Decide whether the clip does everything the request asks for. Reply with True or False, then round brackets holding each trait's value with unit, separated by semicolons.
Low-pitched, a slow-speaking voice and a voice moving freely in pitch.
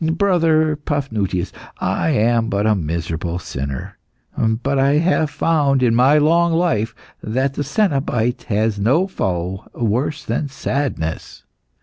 True (130 Hz; 125 wpm; 6.5 semitones)